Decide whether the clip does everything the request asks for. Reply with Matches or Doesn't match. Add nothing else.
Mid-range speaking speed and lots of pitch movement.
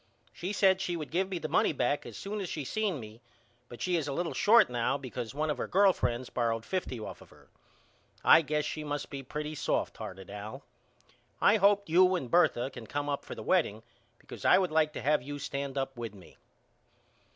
Doesn't match